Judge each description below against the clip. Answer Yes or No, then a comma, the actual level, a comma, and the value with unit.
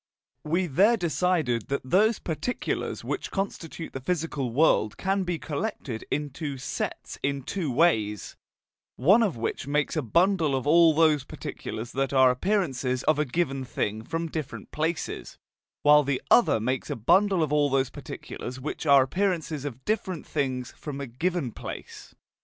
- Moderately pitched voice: Yes, medium, 150 Hz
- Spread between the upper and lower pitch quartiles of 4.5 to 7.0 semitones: Yes, average, 4.8 semitones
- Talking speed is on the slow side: No, average, 160 wpm